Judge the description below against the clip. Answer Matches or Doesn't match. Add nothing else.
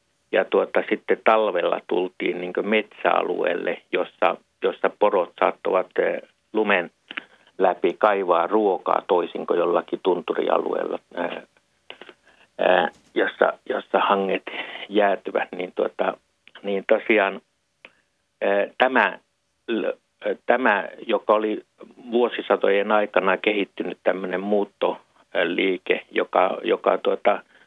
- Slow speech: Matches